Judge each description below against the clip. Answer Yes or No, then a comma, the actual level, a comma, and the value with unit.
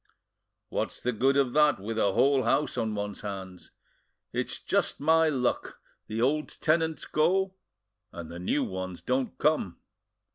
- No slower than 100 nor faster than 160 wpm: Yes, average, 150 wpm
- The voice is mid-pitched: No, low, 125 Hz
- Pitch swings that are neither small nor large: No, wide, 6.9 semitones